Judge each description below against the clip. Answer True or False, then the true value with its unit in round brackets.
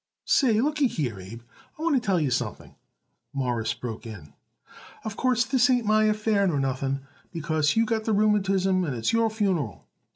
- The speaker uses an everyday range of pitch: False (8.8 semitones)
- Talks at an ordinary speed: True (175 wpm)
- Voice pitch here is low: False (195 Hz)